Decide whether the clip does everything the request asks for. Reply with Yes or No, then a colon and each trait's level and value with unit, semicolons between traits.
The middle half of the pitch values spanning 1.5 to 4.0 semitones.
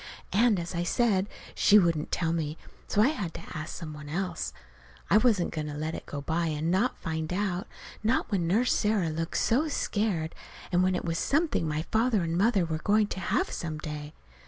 No: average, 4.8 semitones